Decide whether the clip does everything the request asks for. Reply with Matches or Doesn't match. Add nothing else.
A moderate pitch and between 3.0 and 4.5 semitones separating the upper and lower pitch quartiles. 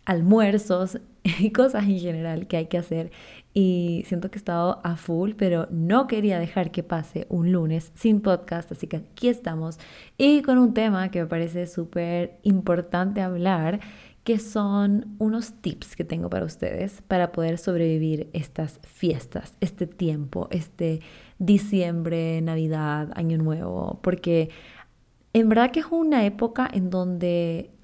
Matches